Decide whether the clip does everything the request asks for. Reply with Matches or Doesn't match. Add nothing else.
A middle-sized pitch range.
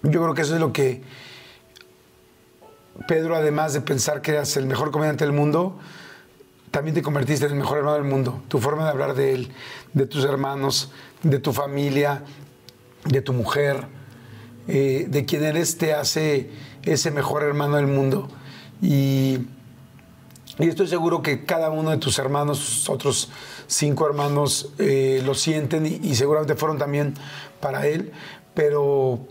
Doesn't match